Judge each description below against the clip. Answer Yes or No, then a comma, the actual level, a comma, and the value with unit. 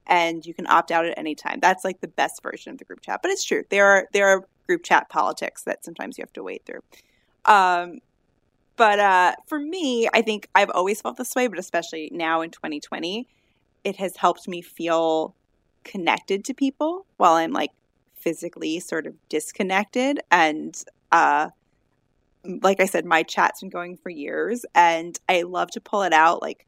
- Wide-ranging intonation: Yes, wide, 6.0 semitones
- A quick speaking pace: No, average, 190 wpm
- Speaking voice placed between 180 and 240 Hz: Yes, high, 190 Hz